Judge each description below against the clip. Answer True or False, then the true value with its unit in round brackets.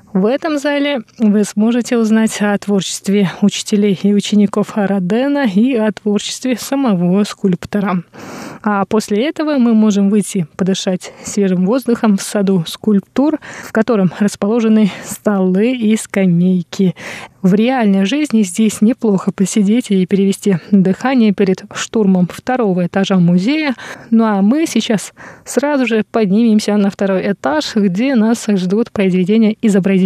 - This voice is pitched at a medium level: False (210 Hz)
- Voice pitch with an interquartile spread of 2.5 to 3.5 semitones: True (2.9 semitones)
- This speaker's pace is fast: False (130 wpm)